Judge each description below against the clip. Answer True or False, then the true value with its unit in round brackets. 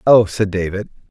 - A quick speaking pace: False (165 wpm)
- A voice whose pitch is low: True (105 Hz)